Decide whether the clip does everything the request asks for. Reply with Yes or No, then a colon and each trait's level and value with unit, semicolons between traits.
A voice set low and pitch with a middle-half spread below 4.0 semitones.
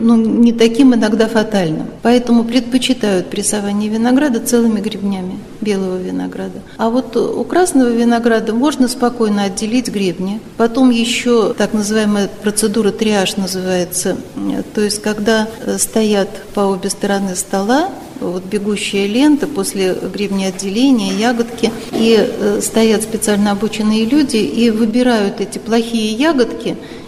No: high, 220 Hz; average, 2.8 semitones